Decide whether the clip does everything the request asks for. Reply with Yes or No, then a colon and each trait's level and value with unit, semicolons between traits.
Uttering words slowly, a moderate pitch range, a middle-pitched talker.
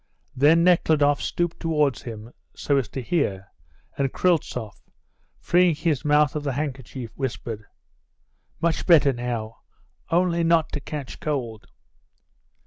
Yes: slow, 125 wpm; average, 4.9 semitones; medium, 145 Hz